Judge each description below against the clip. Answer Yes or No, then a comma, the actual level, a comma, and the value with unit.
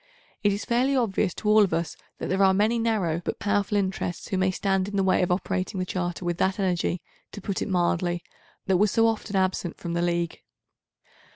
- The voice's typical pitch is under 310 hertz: Yes, high, 190 Hz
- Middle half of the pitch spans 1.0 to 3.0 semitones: Yes, narrow, 2.6 semitones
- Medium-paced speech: No, fast, 215 wpm